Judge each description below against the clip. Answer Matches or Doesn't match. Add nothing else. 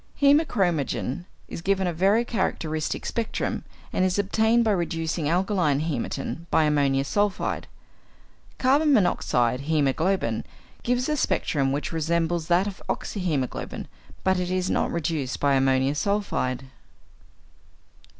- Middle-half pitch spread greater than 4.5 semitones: Matches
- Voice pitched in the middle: Matches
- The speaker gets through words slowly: Matches